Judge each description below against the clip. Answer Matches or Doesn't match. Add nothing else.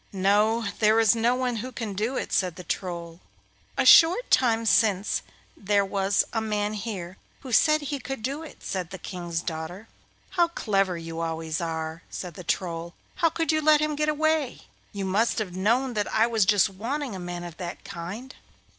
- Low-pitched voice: Doesn't match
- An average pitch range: Doesn't match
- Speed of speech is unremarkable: Matches